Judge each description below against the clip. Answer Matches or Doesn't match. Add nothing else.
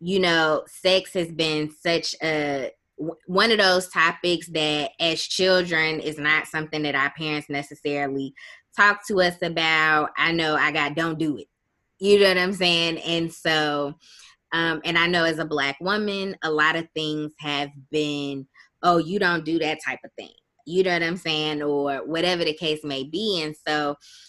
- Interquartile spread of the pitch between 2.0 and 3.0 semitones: Matches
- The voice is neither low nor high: Matches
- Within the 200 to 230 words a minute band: Doesn't match